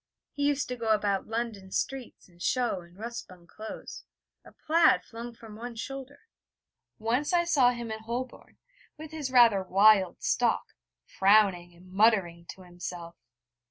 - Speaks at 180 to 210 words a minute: No, average, 155 wpm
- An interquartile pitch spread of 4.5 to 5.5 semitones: Yes, average, 4.8 semitones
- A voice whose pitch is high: Yes, high, 220 Hz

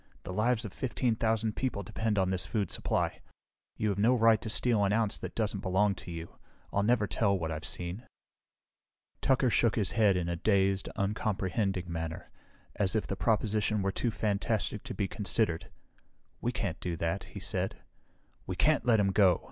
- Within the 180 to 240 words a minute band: Yes, average, 185 wpm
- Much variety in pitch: No, average, 2.9 semitones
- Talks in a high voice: No, low, 100 Hz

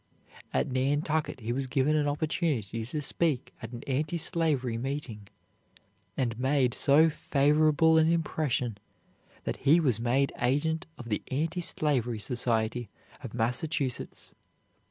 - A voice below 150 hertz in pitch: Yes, low, 135 Hz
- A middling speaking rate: No, slow, 130 wpm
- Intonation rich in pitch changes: No, average, 4.2 semitones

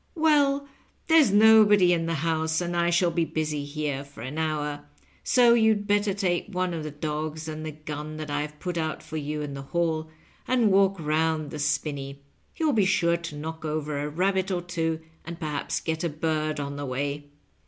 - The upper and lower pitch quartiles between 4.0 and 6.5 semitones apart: No, average, 3.5 semitones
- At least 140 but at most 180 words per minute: No, average, 195 wpm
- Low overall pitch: No, medium, 160 Hz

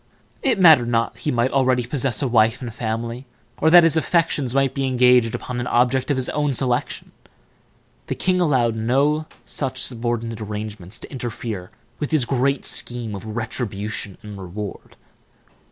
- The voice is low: Yes, low, 120 Hz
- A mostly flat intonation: No, average, 3.4 semitones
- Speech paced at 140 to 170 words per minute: Yes, average, 165 wpm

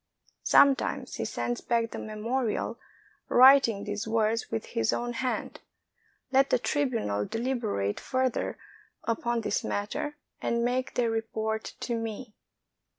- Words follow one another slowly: Yes, slow, 125 wpm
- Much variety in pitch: No, average, 2.8 semitones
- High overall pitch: Yes, high, 230 Hz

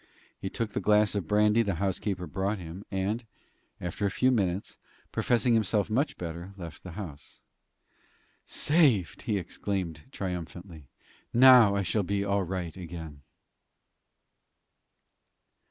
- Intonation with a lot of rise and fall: No, average, 3.3 semitones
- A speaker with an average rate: No, slow, 125 wpm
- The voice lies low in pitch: Yes, low, 100 Hz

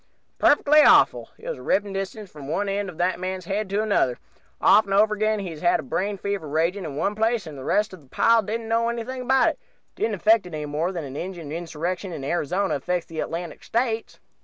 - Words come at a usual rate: No, fast, 230 wpm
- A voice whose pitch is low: No, high, 195 Hz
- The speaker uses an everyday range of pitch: Yes, average, 4.5 semitones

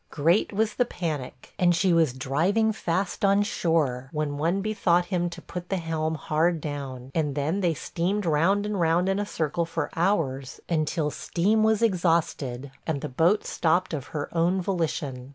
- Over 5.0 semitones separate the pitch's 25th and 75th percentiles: No, average, 4.1 semitones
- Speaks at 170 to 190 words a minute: Yes, average, 175 wpm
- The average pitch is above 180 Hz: No, medium, 165 Hz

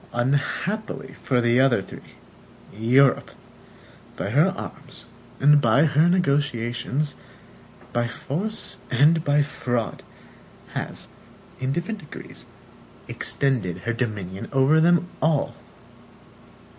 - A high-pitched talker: No, low, 135 Hz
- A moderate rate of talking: No, slow, 100 wpm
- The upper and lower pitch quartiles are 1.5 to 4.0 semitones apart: No, average, 4.4 semitones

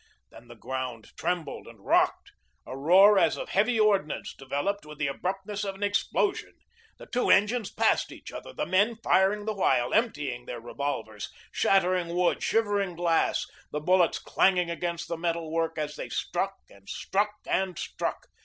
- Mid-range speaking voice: Yes, medium, 175 Hz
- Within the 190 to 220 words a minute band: No, average, 165 wpm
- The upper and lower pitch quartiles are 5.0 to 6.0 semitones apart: Yes, wide, 5.4 semitones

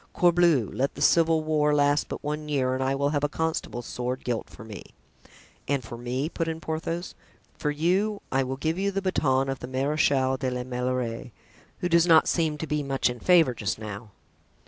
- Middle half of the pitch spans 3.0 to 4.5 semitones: Yes, average, 4.1 semitones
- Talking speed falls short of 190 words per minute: No, fast, 205 wpm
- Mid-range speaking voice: Yes, medium, 145 Hz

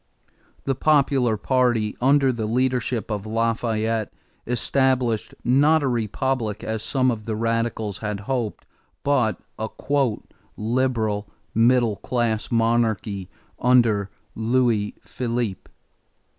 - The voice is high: No, low, 115 Hz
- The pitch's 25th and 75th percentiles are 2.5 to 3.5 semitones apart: Yes, average, 2.8 semitones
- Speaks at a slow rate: Yes, slow, 105 wpm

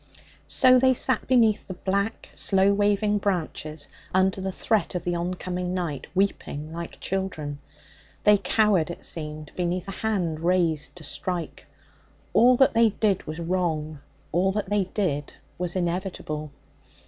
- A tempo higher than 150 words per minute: No, average, 145 wpm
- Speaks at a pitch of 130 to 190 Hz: Yes, medium, 185 Hz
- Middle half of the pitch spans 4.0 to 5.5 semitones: No, average, 3.4 semitones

